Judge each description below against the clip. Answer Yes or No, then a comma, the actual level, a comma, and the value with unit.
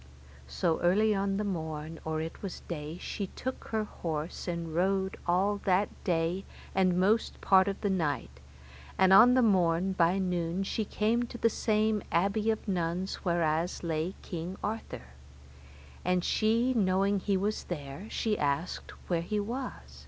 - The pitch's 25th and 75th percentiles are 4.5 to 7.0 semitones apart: No, average, 3.8 semitones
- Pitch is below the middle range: No, medium, 185 Hz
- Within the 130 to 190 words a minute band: Yes, average, 160 wpm